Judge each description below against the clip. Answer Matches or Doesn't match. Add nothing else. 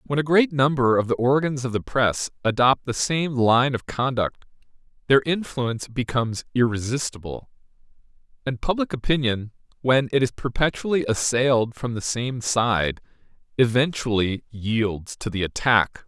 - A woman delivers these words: Doesn't match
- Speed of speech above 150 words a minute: Doesn't match